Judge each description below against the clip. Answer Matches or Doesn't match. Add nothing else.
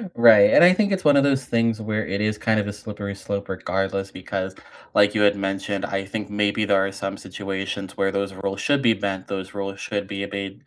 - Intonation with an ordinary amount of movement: Doesn't match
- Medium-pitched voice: Doesn't match